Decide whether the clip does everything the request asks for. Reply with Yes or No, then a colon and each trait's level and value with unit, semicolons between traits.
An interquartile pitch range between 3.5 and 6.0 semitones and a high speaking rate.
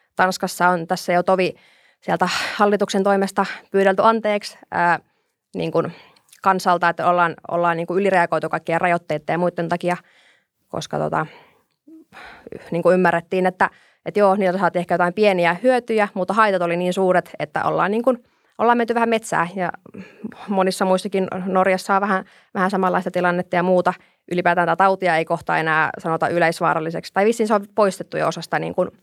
No: narrow, 2.5 semitones; fast, 160 wpm